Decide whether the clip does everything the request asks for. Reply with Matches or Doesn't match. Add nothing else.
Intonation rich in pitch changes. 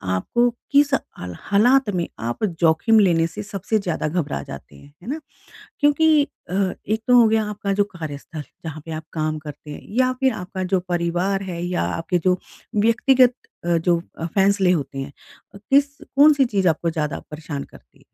Matches